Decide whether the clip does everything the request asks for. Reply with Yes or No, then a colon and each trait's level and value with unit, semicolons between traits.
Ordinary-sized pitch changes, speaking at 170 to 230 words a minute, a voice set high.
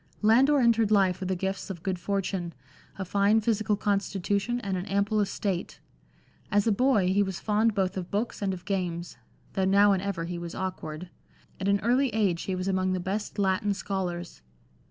No: narrow, 2.1 semitones; average, 190 wpm; high, 195 Hz